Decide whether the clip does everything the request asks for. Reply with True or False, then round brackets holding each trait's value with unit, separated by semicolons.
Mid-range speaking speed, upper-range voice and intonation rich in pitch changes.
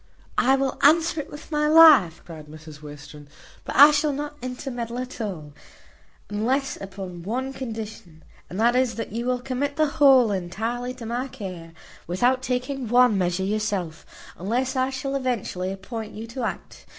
True (170 wpm; 240 Hz; 5.7 semitones)